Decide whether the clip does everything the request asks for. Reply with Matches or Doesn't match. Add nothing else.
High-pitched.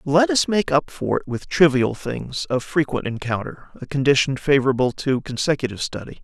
Doesn't match